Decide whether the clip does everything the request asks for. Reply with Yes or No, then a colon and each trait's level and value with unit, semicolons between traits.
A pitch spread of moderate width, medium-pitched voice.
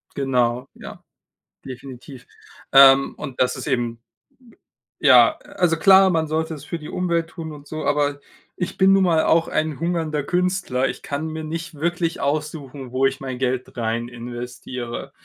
Yes: average, 4.3 semitones; medium, 145 Hz